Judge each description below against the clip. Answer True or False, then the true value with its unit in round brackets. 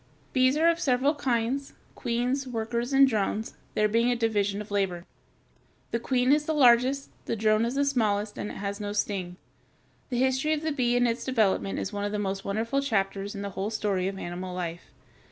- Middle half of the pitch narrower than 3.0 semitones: False (4.3 semitones)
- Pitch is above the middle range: True (225 Hz)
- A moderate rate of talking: False (210 wpm)